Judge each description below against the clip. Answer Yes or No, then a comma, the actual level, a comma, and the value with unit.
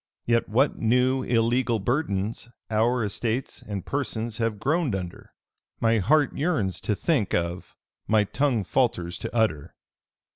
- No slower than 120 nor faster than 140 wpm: Yes, slow, 135 wpm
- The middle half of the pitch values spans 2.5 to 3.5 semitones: No, average, 3.9 semitones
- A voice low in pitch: Yes, low, 115 Hz